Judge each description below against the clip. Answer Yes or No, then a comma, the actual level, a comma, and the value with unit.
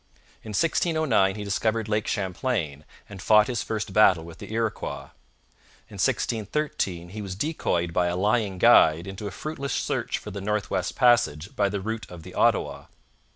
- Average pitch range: Yes, average, 3.5 semitones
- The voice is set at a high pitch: No, low, 105 Hz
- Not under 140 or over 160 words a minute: No, average, 170 wpm